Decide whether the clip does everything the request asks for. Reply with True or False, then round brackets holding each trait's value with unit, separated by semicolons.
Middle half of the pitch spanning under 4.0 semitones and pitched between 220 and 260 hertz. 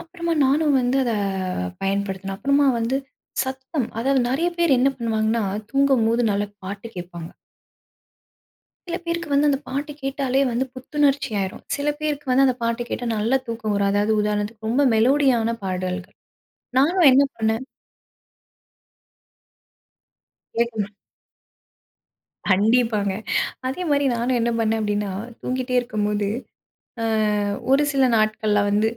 False (4.5 semitones; 240 Hz)